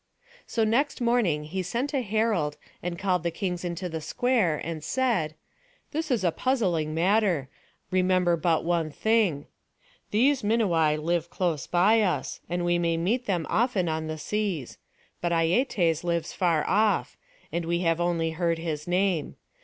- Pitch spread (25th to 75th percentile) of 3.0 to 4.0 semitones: No, average, 4.6 semitones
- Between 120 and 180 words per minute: Yes, average, 160 wpm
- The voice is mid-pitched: Yes, medium, 175 Hz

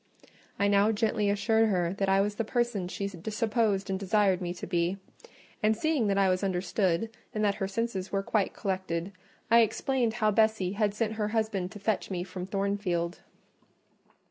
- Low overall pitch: No, high, 200 Hz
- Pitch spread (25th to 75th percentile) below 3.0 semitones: Yes, narrow, 2.6 semitones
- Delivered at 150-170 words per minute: No, average, 180 wpm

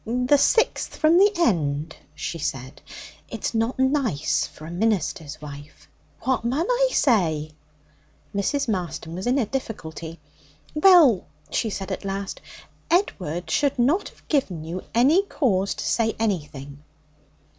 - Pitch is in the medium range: No, high, 210 Hz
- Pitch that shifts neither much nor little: No, wide, 8.9 semitones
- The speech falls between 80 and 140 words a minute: Yes, slow, 135 wpm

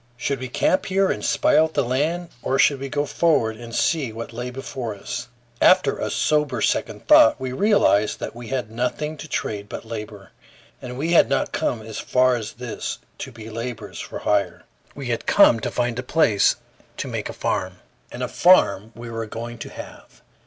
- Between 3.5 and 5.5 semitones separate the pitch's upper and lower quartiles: Yes, average, 4.3 semitones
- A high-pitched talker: No, low, 125 Hz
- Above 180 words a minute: Yes, average, 200 wpm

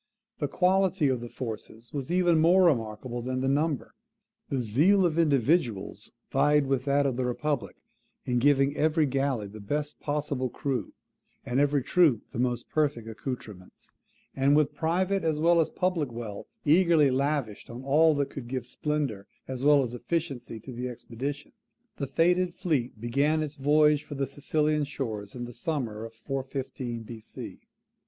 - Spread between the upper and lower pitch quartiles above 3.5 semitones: Yes, average, 3.9 semitones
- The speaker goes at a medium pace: Yes, average, 160 wpm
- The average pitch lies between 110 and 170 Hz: Yes, medium, 140 Hz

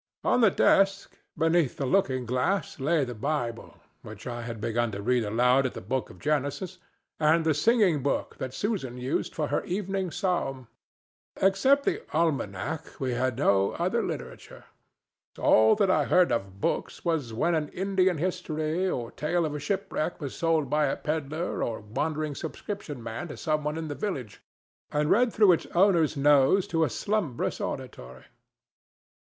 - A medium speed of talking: Yes, average, 165 wpm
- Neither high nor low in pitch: Yes, medium, 150 Hz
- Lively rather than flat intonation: Yes, wide, 5.8 semitones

